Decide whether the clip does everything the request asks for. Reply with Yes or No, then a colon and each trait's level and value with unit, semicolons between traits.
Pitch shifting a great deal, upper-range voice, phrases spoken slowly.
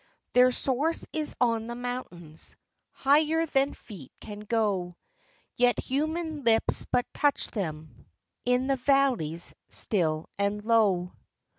Yes: wide, 5.7 semitones; high, 240 Hz; slow, 120 wpm